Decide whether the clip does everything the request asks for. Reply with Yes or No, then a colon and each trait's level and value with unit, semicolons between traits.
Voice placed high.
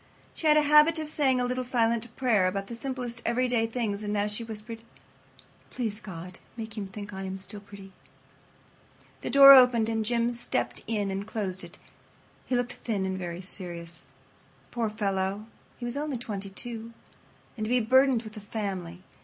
Yes: high, 220 Hz